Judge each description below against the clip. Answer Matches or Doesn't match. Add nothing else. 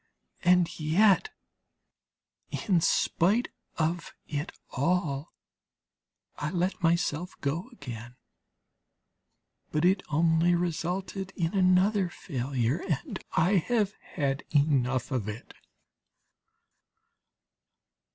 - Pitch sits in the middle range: Matches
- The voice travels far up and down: Doesn't match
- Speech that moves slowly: Matches